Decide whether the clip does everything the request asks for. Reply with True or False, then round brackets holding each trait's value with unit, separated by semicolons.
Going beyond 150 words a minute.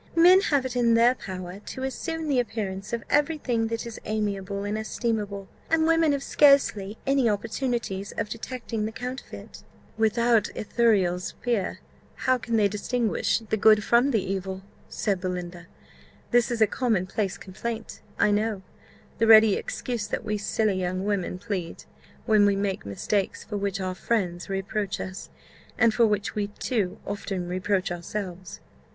True (160 wpm)